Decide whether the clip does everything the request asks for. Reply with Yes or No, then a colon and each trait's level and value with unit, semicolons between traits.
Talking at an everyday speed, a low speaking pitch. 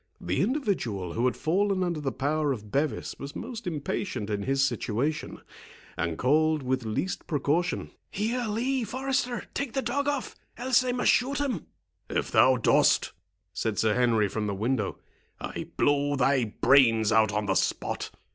No: average, 155 wpm; medium, 145 Hz